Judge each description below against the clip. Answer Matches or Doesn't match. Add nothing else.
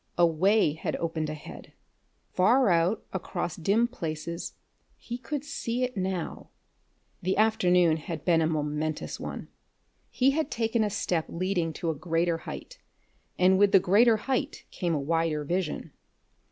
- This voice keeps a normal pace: Matches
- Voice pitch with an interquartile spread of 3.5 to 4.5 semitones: Doesn't match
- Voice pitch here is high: Doesn't match